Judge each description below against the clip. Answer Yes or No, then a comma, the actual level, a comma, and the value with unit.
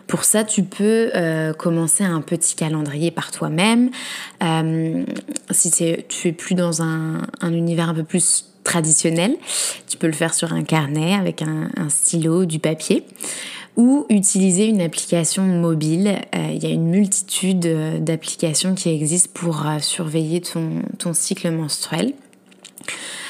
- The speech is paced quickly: No, average, 150 wpm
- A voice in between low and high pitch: Yes, medium, 170 Hz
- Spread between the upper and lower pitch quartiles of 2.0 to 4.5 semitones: Yes, average, 3.6 semitones